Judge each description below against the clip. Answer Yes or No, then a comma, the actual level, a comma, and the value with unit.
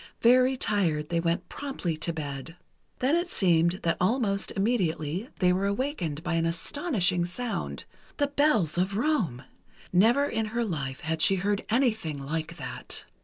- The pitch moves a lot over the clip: Yes, wide, 6.4 semitones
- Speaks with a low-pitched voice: No, medium, 185 Hz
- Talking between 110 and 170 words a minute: Yes, average, 150 wpm